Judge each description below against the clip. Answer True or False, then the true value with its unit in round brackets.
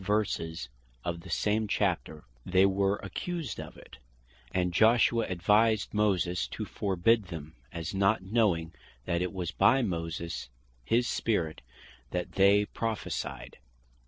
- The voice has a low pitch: True (95 Hz)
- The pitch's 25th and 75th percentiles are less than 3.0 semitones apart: False (4.0 semitones)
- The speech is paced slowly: True (130 wpm)